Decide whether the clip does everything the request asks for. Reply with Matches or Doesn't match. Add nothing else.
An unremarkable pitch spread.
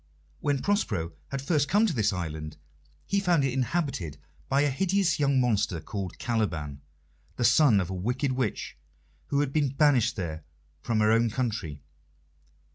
Doesn't match